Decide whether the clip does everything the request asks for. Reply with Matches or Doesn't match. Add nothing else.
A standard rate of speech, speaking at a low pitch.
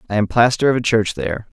Doesn't match